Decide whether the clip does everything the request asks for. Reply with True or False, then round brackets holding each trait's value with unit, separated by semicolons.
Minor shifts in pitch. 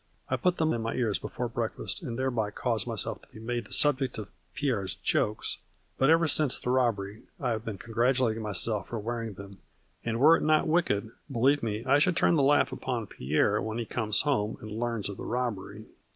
False (3.7 semitones)